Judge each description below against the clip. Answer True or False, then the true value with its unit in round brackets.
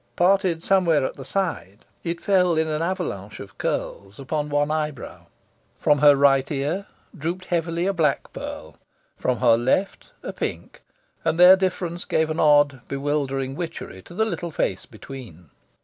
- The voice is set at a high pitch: False (155 Hz)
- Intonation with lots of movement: False (4.3 semitones)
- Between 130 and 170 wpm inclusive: True (160 wpm)